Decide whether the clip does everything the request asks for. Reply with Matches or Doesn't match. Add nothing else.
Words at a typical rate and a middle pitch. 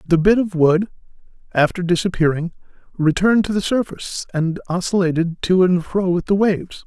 Matches